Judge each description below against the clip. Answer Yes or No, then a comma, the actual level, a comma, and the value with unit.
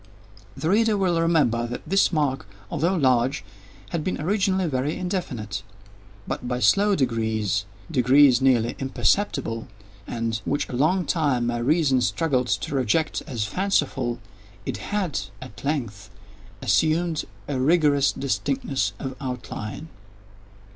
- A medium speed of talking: No, slow, 120 wpm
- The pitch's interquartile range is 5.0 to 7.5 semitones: Yes, wide, 5.6 semitones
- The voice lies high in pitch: No, low, 135 Hz